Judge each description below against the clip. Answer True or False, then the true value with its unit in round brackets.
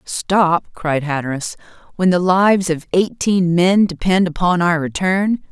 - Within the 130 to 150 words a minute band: True (140 wpm)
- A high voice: False (180 Hz)